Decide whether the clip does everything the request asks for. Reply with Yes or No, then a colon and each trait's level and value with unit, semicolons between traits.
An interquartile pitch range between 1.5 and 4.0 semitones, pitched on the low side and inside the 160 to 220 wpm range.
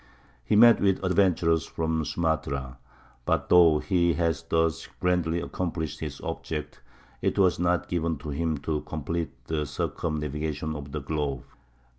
No: narrow, 2.4 semitones; very low, 80 Hz; average, 140 wpm